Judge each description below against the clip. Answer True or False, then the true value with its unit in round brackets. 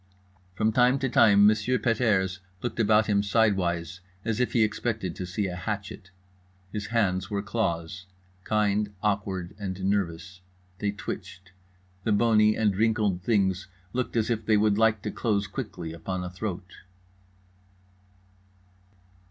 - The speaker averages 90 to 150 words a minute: True (145 wpm)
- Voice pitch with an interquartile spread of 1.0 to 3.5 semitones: True (2.7 semitones)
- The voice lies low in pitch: True (105 Hz)